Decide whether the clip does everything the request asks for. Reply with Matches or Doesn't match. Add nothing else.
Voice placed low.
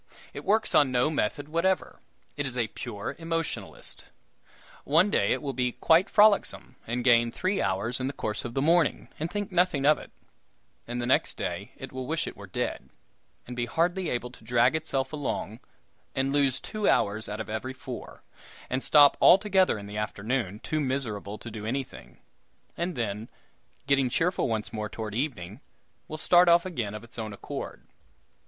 Matches